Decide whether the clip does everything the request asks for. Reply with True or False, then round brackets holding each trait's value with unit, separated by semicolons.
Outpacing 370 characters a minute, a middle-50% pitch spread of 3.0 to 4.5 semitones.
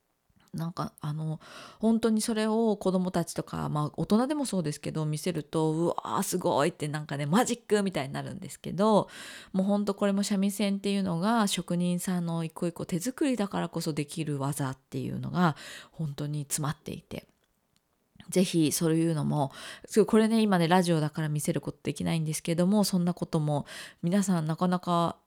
True (380 characters per minute; 4.1 semitones)